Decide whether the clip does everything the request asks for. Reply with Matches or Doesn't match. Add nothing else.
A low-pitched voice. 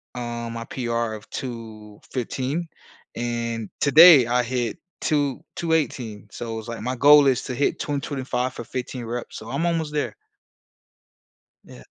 Matches